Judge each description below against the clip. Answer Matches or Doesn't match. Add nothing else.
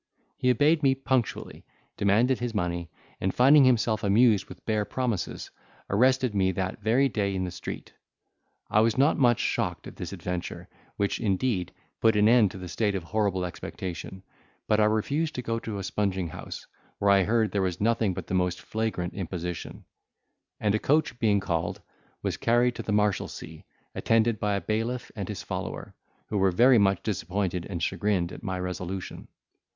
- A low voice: Matches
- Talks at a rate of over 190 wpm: Doesn't match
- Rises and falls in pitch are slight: Doesn't match